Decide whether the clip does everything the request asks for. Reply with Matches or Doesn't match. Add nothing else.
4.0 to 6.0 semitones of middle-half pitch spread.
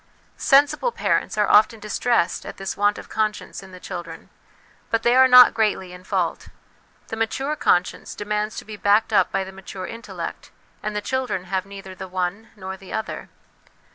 Doesn't match